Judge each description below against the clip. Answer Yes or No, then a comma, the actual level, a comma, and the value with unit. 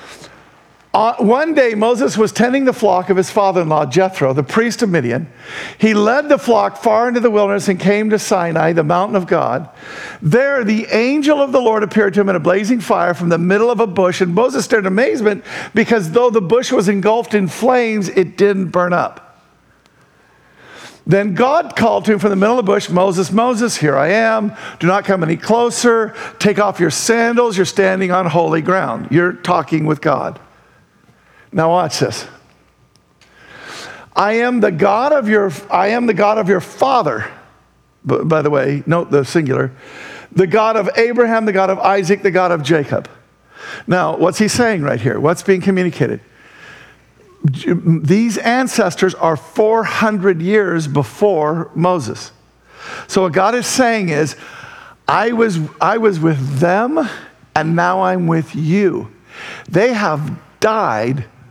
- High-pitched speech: Yes, high, 195 Hz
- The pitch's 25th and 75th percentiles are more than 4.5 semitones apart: Yes, average, 4.9 semitones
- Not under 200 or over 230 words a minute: No, average, 170 wpm